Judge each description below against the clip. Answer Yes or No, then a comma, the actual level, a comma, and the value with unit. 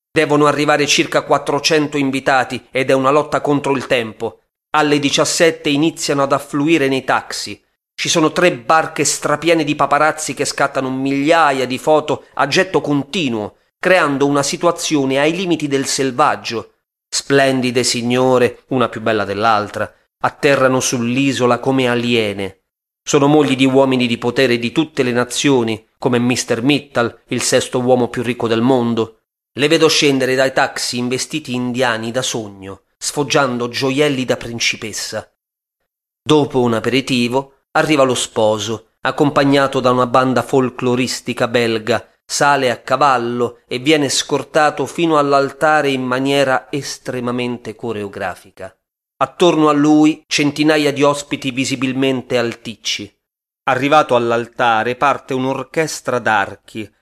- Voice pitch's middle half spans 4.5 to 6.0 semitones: No, average, 3.2 semitones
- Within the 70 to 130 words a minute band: Yes, average, 125 wpm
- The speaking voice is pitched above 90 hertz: Yes, low, 135 Hz